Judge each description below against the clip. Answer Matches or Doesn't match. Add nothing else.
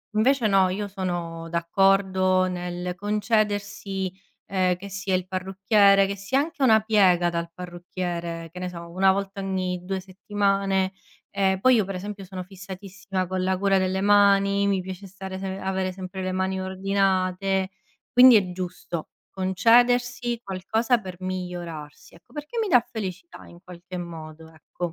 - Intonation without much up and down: Matches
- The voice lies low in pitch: Doesn't match